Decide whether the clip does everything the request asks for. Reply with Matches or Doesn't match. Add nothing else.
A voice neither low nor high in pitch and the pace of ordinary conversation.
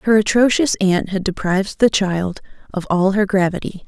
Doesn't match